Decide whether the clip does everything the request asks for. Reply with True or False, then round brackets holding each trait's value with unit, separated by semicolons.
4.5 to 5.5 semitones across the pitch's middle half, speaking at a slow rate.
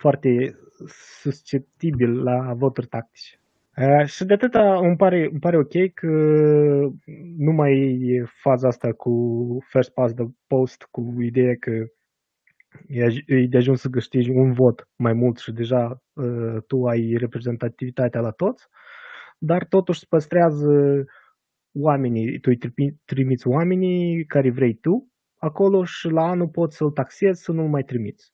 False (4.8 semitones; 150 wpm)